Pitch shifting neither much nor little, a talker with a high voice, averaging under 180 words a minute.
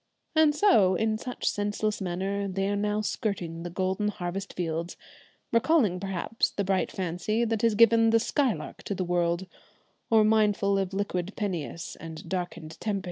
Yes: average, 3.3 semitones; high, 200 Hz; average, 160 wpm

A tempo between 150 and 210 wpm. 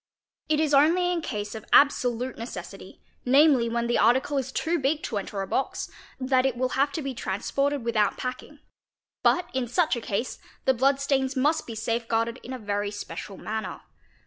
Yes: average, 195 wpm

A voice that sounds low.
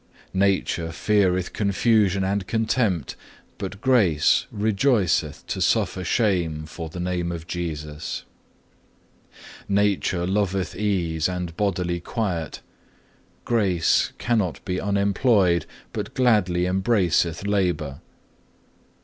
Yes: very low, 95 Hz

